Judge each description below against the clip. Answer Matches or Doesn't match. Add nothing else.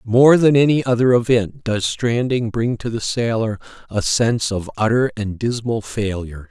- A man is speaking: Matches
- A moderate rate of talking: Matches